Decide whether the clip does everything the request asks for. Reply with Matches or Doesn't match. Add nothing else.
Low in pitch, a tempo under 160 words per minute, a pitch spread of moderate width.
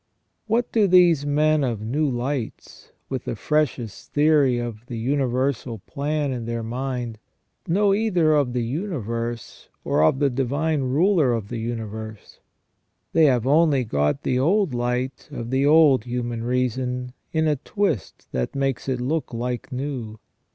Matches